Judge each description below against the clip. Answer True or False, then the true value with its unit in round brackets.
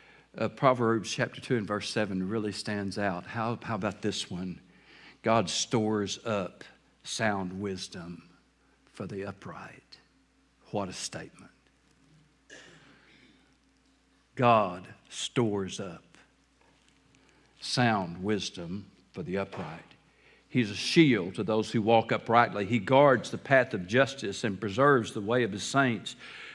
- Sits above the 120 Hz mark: False (105 Hz)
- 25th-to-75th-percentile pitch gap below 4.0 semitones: True (3.5 semitones)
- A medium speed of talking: False (125 wpm)